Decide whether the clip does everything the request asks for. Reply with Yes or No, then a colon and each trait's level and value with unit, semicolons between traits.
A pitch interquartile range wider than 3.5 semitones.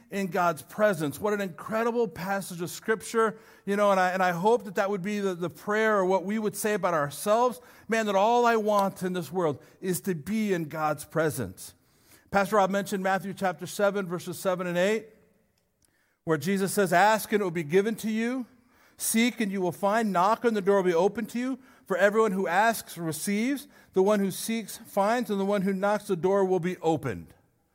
No: average, 3.2 semitones